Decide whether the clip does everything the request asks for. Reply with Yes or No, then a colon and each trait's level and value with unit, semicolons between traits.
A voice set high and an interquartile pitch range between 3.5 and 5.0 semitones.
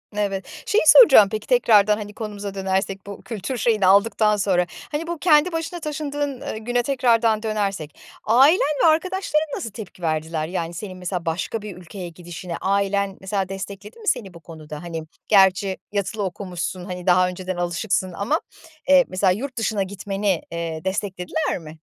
Yes: high, 200 Hz; average, 4.1 semitones